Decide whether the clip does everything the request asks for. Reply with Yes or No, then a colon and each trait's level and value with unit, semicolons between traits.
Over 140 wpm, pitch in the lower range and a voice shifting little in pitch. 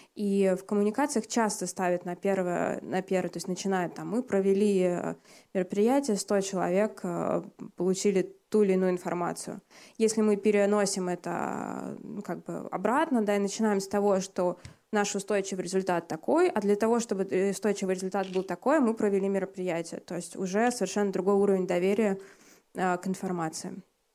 No: average, 150 wpm; high, 195 Hz; narrow, 2.1 semitones